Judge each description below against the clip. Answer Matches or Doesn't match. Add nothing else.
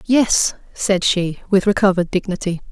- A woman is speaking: Matches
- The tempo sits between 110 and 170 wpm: Matches